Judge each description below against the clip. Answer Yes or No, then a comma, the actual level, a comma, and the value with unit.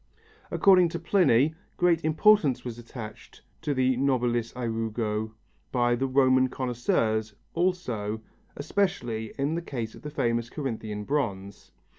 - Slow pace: Yes, slow, 125 wpm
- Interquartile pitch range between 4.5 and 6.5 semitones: Yes, average, 4.9 semitones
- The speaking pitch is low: Yes, low, 125 Hz